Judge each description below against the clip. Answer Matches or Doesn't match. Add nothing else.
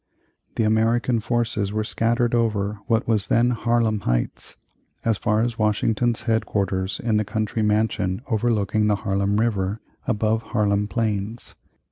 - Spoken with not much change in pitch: Matches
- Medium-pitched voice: Doesn't match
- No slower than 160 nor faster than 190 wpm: Doesn't match